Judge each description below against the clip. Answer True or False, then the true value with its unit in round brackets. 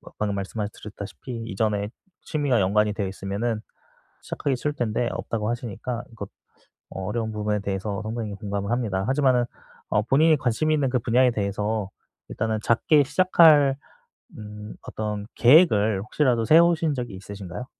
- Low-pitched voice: True (110 Hz)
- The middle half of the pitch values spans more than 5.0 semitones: False (3.8 semitones)